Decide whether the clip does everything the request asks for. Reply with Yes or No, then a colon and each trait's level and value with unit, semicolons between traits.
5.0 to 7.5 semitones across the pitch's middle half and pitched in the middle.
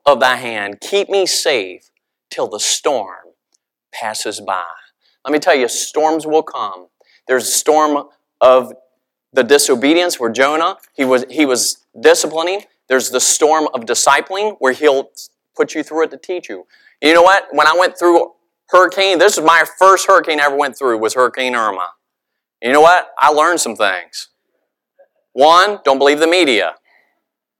Yes: average, 5.3 semitones; medium, 155 Hz